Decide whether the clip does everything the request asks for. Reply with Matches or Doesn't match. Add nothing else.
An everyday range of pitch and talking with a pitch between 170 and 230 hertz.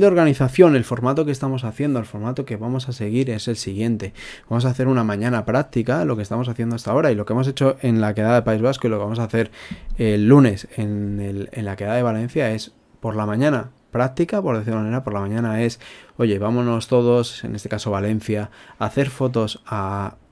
Doesn't match